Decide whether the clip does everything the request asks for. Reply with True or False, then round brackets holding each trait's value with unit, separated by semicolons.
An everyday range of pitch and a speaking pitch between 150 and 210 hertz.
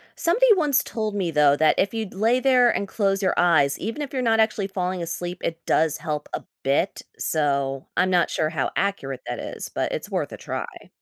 False (6.2 semitones; 185 Hz)